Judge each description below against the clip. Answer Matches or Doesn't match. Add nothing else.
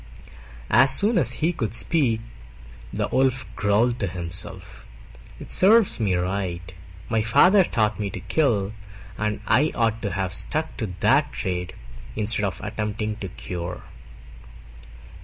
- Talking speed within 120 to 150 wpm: Matches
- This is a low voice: Matches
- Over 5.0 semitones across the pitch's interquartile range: Matches